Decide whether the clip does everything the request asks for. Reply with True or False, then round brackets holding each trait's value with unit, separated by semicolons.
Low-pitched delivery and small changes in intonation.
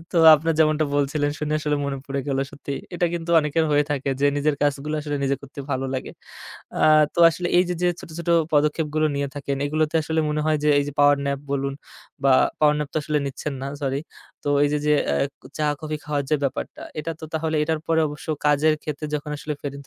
False (150 Hz; 1.5 semitones)